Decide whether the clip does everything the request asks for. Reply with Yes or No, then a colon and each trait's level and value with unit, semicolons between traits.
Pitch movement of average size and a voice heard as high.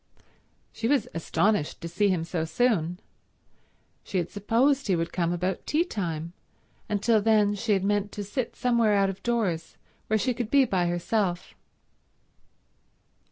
Yes: average, 4.5 semitones; high, 205 Hz